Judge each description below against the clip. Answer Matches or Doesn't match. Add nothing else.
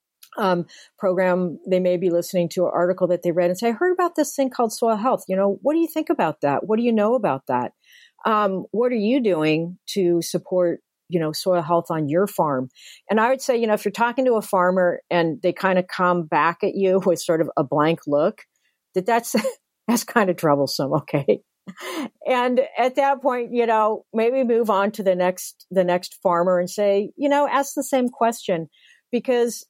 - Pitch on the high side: Matches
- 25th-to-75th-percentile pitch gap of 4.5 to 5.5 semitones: Matches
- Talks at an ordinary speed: Doesn't match